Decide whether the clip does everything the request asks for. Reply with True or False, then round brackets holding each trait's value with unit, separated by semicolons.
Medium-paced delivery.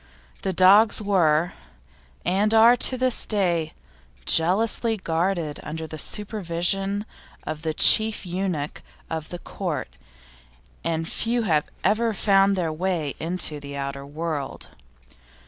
False (120 wpm)